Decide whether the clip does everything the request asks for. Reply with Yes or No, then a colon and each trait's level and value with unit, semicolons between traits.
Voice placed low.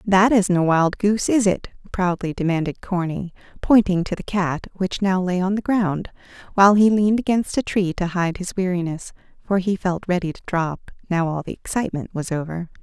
No: medium, 185 Hz